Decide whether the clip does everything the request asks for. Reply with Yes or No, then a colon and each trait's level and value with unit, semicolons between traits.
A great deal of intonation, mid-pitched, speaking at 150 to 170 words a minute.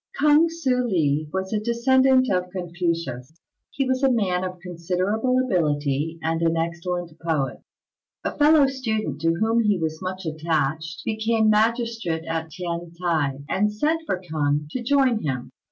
Yes: wide, 6.2 semitones; medium, 180 Hz; average, 155 wpm